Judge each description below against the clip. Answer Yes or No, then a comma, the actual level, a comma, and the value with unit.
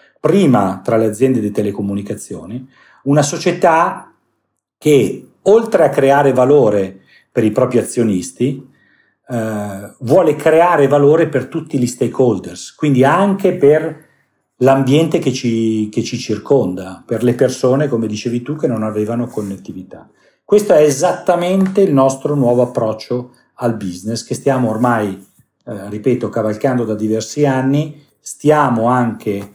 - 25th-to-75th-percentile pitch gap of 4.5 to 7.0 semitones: Yes, average, 4.8 semitones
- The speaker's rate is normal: Yes, average, 130 wpm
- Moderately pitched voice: No, low, 125 Hz